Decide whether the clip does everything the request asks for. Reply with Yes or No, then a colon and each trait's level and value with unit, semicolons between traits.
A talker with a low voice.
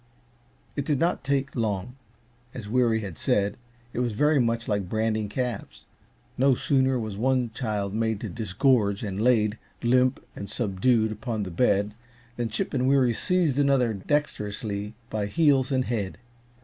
Yes: low, 115 Hz